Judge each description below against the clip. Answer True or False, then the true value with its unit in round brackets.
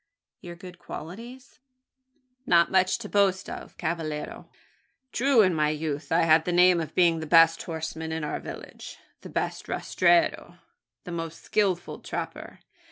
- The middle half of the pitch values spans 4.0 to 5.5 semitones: False (2.8 semitones)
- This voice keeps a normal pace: True (150 wpm)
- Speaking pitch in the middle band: True (170 Hz)